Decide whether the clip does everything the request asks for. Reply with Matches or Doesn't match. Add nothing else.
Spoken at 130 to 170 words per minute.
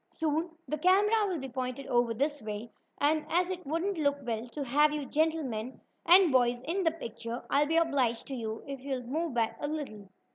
Doesn't match